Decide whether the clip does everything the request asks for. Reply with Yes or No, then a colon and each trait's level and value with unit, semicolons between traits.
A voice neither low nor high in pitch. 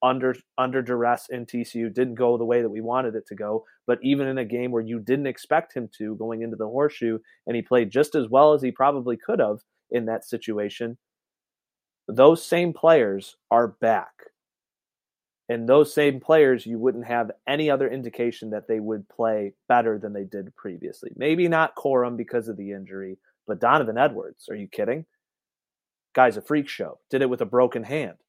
No: low, 120 Hz